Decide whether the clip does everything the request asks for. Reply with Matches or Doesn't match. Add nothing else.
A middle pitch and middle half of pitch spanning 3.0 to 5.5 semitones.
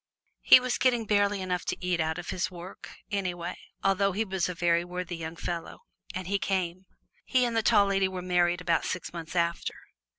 Doesn't match